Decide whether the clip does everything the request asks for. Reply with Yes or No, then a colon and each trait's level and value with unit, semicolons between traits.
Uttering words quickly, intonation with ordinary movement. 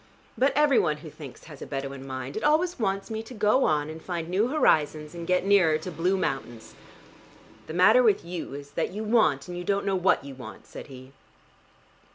No: fast, 210 wpm; wide, 6.2 semitones